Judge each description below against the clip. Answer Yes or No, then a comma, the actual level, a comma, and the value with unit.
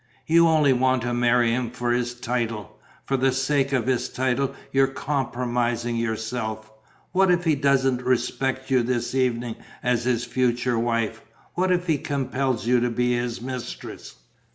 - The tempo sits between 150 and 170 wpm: Yes, average, 160 wpm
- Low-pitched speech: Yes, low, 125 Hz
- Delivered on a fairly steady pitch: Yes, narrow, 2.0 semitones